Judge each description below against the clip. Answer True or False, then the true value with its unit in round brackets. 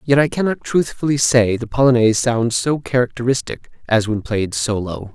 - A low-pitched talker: True (120 Hz)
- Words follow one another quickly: False (165 wpm)